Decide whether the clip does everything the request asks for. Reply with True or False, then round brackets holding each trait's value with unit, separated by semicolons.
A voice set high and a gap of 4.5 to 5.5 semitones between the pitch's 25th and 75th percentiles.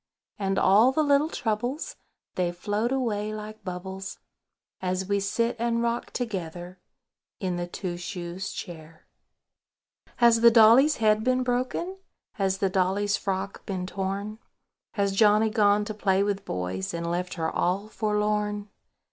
False (205 Hz; 3.1 semitones)